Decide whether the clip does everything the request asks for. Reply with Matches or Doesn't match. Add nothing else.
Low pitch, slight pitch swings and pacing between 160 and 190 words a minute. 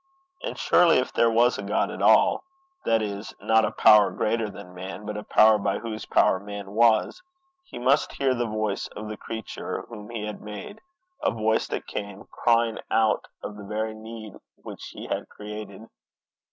Matches